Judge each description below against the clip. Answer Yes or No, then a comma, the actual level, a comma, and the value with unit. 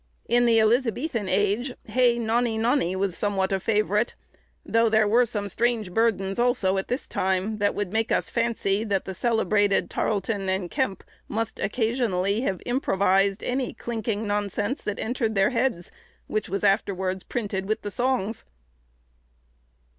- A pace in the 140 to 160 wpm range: Yes, average, 150 wpm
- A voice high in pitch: Yes, high, 215 Hz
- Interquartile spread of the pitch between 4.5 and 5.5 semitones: No, average, 3.3 semitones